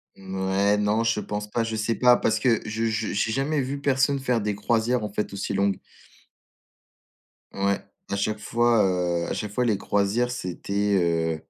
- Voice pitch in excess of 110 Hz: No, low, 105 Hz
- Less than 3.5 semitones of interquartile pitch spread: Yes, average, 3.0 semitones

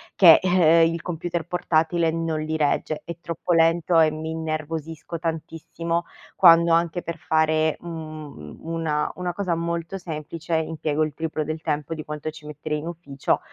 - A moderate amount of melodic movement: No, narrow, 1.3 semitones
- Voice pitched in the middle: Yes, medium, 160 Hz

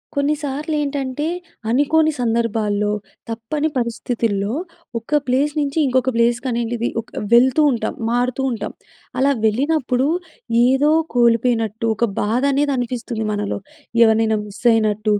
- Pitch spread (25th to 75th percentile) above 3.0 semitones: Yes, average, 3.6 semitones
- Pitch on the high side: Yes, high, 240 Hz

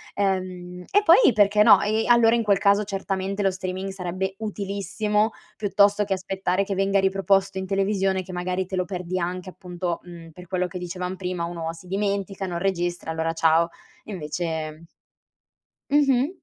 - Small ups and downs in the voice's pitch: Yes, narrow, 2.0 semitones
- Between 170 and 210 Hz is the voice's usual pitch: Yes, high, 190 Hz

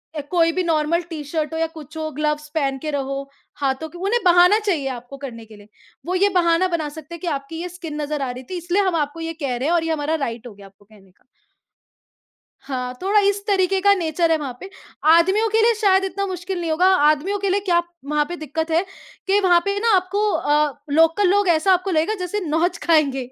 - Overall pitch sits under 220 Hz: No, very high, 325 Hz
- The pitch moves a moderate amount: Yes, average, 4.0 semitones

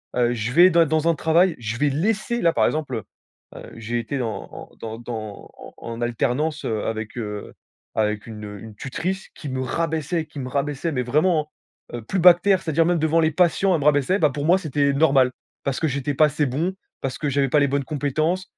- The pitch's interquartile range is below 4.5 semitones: No, average, 5.1 semitones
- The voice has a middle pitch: Yes, medium, 145 Hz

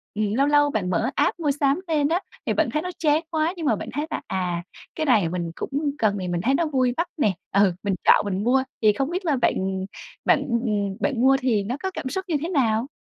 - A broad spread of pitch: Yes, wide, 6.7 semitones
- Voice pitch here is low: No, very high, 255 Hz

